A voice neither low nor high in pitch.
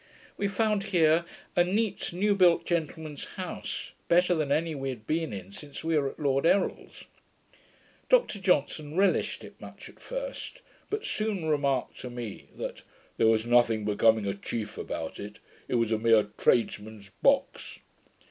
Yes: medium, 150 Hz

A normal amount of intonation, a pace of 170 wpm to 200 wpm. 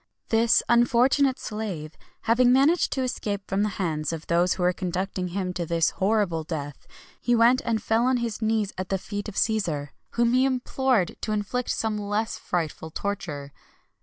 Yes: average, 4.9 semitones; average, 175 wpm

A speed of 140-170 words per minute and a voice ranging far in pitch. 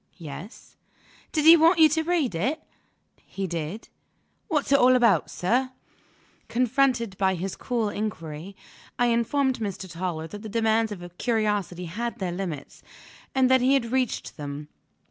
Yes: average, 150 wpm; wide, 6.0 semitones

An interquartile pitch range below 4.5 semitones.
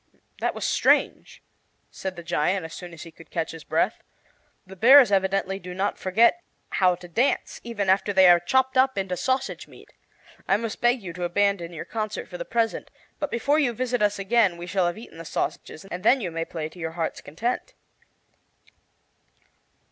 No: average, 5.1 semitones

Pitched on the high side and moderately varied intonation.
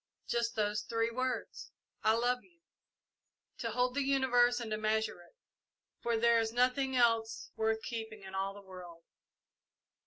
No: high, 230 Hz; narrow, 2.3 semitones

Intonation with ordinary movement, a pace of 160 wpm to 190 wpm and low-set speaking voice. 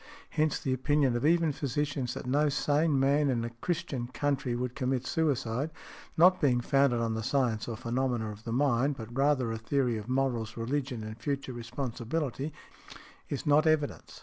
Yes: average, 3.5 semitones; average, 175 wpm; low, 130 Hz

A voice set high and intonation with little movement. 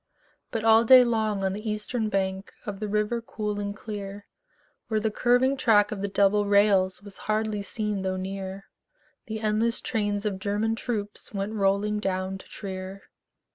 Yes: high, 205 Hz; narrow, 1.8 semitones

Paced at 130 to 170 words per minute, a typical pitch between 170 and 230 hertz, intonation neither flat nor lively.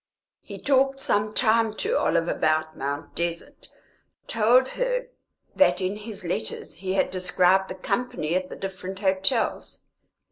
Yes: average, 140 wpm; high, 190 Hz; average, 4.4 semitones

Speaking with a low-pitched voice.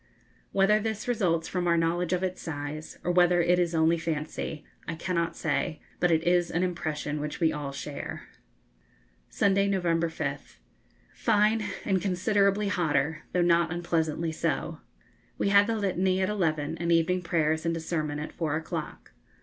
No: medium, 170 Hz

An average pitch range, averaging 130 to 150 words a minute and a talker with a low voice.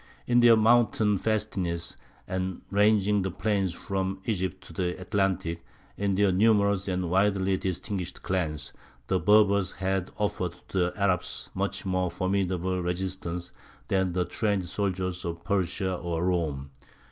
No: narrow, 2.1 semitones; average, 140 wpm; very low, 95 Hz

